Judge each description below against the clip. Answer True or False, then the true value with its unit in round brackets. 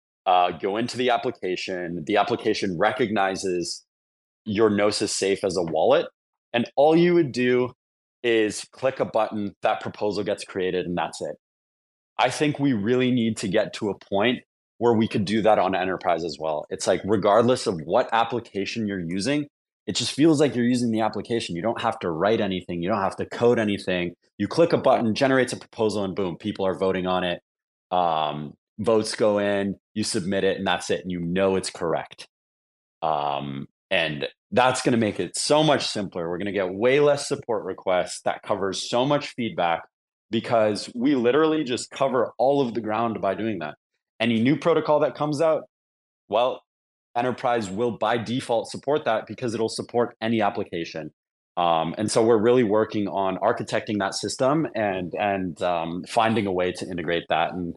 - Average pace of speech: True (185 wpm)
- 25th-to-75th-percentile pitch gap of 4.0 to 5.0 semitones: True (4.3 semitones)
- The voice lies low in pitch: True (110 Hz)